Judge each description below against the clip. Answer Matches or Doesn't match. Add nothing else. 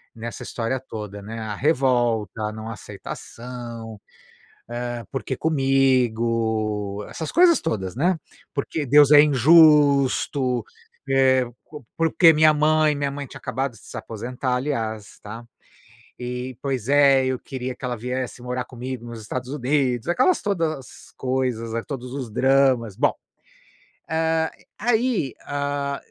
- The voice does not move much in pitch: Doesn't match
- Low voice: Matches